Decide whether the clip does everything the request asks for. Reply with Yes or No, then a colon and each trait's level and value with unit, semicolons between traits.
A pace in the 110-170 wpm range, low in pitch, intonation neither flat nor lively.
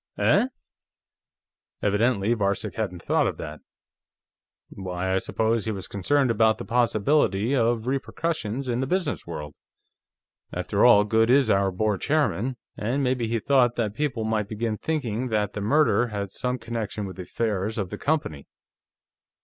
Yes: average, 155 wpm; low, 110 Hz; average, 3.8 semitones